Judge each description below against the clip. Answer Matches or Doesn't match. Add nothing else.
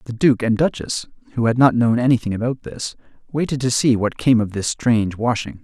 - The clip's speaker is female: Doesn't match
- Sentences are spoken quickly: Matches